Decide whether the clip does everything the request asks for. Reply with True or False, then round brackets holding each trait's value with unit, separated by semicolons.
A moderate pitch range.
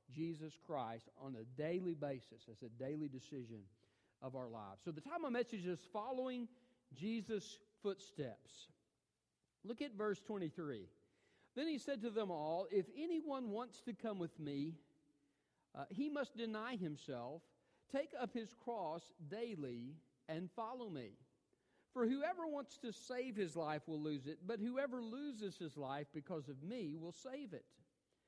False (8.3 semitones)